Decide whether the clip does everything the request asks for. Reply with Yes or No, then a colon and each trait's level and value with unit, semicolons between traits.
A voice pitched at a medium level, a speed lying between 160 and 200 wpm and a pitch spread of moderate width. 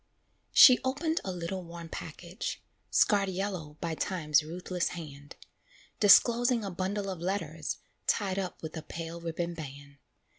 No: medium, 175 Hz; average, 140 wpm; average, 3.5 semitones